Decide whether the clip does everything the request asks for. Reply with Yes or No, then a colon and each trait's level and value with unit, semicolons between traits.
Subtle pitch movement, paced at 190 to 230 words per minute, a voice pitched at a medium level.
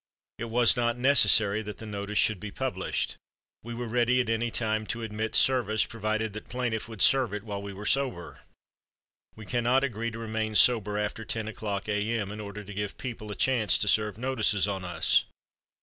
No: narrow, 2.2 semitones; average, 195 wpm; low, 110 Hz